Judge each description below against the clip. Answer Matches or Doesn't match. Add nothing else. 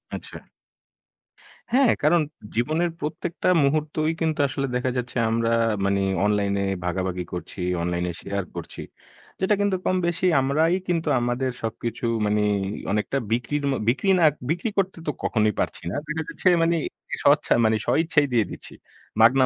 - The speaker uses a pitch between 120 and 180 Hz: Matches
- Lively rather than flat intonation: Matches